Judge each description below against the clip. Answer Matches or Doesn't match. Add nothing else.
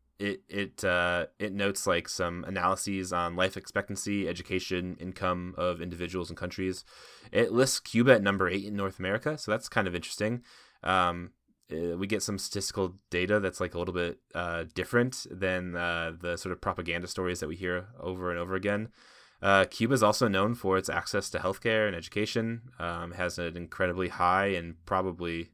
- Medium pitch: Doesn't match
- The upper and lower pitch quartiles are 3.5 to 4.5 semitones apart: Doesn't match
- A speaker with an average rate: Matches